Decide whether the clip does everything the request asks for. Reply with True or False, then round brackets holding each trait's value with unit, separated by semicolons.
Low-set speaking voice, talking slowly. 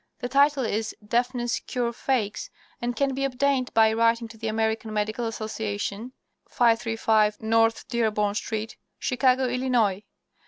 False (230 Hz; 130 wpm)